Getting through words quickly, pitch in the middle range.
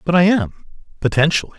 No: average, 150 wpm; medium, 160 Hz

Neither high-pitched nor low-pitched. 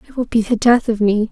No: high, 225 Hz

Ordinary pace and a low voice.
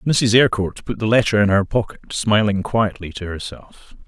Yes: average, 175 wpm; low, 105 Hz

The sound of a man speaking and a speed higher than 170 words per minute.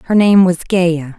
No: female; average, 200 wpm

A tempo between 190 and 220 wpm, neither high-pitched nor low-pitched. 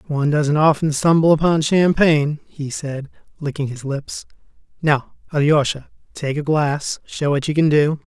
No: average, 155 wpm; medium, 150 Hz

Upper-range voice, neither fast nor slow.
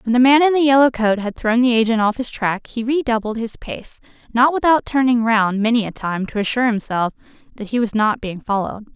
No: high, 230 Hz; fast, 230 wpm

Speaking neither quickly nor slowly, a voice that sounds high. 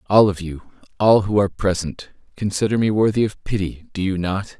No: average, 185 wpm; low, 100 Hz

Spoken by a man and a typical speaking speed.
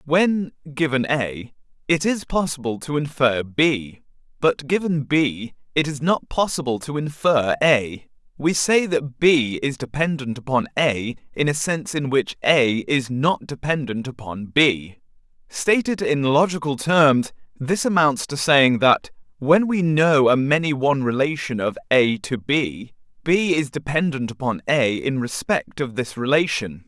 Yes: male; average, 150 wpm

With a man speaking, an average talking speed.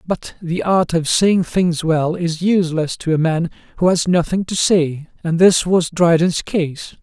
Yes: male; average, 190 wpm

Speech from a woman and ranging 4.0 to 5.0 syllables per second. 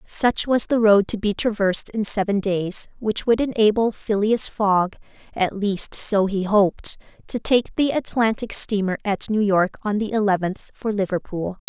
Yes: female; 4.4 syllables/s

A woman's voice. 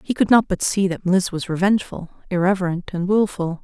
Yes: female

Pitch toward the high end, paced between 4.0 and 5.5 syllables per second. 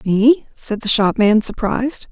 Yes: high, 230 Hz; 4.2 syllables/s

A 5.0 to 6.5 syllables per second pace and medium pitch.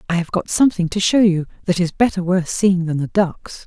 Yes: 5.5 syllables/s; medium, 180 Hz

